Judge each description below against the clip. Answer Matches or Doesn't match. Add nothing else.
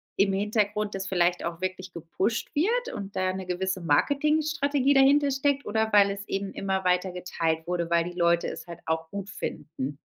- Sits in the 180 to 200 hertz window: Matches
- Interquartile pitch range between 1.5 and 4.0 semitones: Doesn't match